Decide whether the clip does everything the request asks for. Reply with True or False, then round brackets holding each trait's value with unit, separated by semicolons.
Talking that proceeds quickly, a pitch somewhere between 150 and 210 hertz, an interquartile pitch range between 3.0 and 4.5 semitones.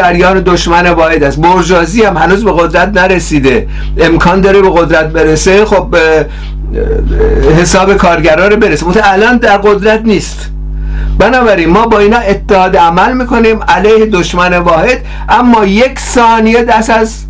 False (140 wpm; 185 Hz; 4.2 semitones)